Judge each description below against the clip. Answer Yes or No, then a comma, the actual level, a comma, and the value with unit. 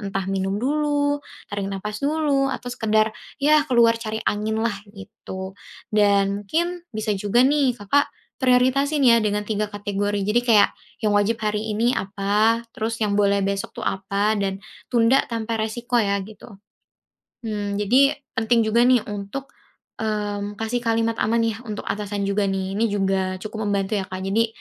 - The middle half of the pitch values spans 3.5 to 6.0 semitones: No, average, 2.8 semitones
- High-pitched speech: Yes, high, 215 Hz